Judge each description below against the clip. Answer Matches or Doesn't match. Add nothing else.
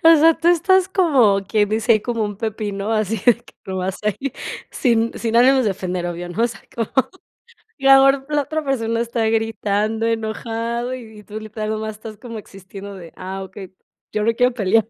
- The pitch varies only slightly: Doesn't match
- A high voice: Matches